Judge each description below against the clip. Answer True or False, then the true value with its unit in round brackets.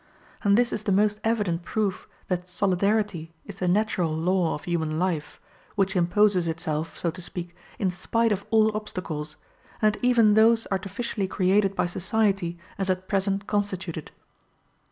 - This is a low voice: False (190 Hz)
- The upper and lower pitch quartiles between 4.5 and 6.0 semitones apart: False (3.2 semitones)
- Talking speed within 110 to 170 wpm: True (155 wpm)